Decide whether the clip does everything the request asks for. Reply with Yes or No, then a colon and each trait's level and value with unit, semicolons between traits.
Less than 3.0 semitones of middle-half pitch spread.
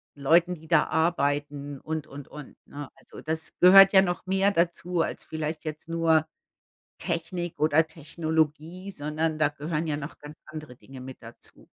Yes: narrow, 2.4 semitones